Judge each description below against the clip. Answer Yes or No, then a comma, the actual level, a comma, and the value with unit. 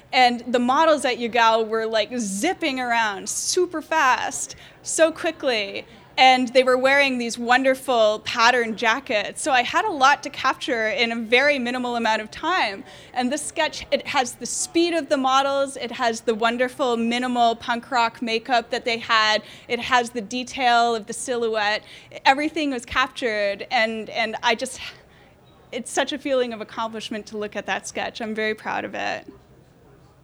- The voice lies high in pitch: Yes, high, 245 Hz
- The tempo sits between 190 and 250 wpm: No, average, 170 wpm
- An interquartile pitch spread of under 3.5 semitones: Yes, average, 2.8 semitones